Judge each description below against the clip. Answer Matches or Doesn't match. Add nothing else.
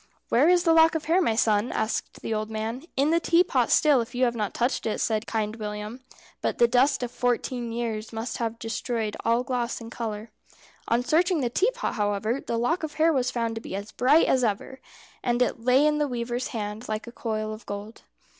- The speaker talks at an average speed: Doesn't match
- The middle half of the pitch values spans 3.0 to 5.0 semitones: Matches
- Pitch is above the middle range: Matches